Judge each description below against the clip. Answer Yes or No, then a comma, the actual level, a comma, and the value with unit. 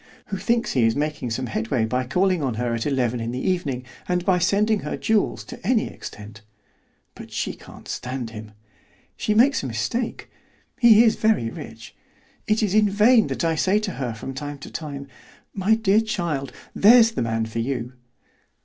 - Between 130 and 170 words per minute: No, average, 185 wpm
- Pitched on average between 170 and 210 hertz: No, medium, 150 Hz